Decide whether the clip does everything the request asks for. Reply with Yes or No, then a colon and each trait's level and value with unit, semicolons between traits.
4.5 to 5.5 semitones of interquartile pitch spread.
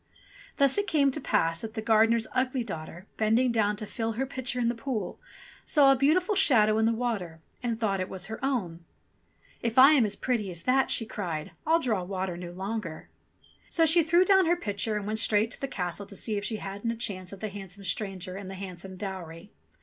Yes: average, 4.8 semitones